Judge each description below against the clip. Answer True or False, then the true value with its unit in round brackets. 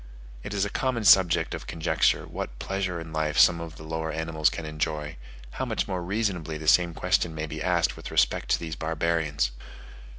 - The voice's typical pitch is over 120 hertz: False (80 Hz)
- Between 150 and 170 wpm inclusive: False (195 wpm)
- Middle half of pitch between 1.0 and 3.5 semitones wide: True (2.4 semitones)